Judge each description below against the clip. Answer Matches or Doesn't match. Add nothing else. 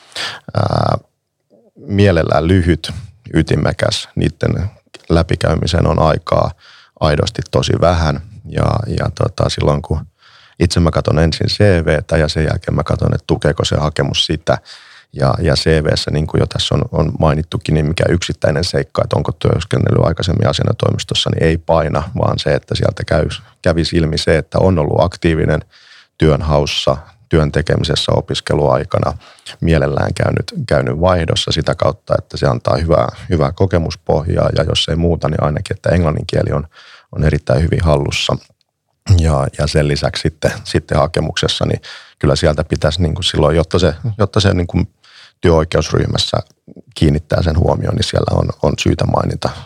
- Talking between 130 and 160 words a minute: Matches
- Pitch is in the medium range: Doesn't match